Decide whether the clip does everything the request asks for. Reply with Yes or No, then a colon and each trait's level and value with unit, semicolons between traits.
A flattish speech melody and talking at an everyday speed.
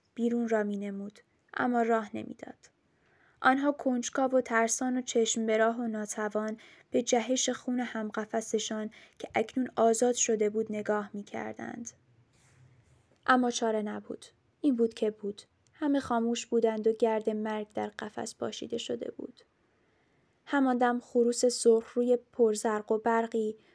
Yes: narrow, 2.2 semitones; average, 140 wpm